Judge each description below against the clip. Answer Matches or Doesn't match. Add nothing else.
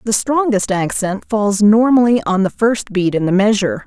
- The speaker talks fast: Doesn't match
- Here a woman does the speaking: Matches